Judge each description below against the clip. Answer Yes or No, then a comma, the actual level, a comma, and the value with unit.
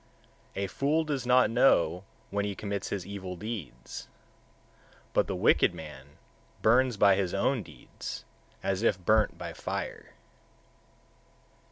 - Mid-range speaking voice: No, low, 100 Hz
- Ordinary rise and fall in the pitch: Yes, average, 4.6 semitones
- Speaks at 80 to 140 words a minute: Yes, slow, 135 wpm